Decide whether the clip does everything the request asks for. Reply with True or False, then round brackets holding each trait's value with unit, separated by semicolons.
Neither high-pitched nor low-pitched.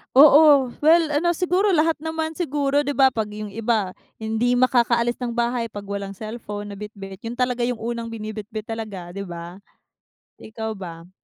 False (235 Hz)